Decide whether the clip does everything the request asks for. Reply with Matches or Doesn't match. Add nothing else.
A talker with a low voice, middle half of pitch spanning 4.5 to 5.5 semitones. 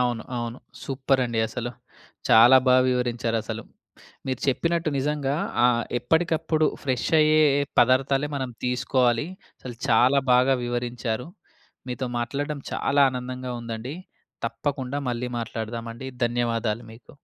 Doesn't match